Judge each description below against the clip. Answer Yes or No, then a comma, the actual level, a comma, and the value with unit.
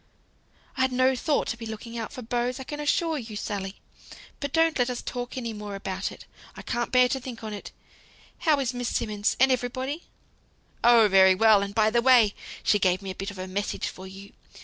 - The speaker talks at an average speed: No, fast, 215 wpm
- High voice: Yes, high, 235 Hz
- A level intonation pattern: No, average, 3.9 semitones